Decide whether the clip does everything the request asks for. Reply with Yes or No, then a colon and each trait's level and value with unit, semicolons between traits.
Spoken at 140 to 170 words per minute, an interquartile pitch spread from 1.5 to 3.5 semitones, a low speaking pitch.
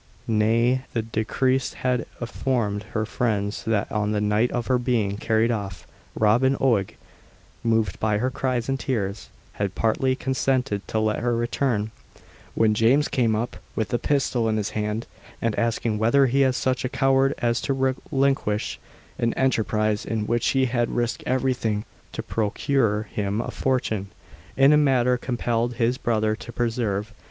Yes: average, 160 wpm; average, 3.2 semitones; low, 115 Hz